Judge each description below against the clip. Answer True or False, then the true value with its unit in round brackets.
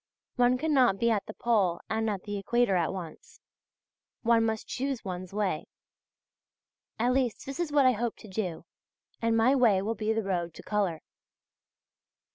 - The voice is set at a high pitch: True (220 Hz)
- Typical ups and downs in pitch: True (3.9 semitones)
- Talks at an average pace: True (170 wpm)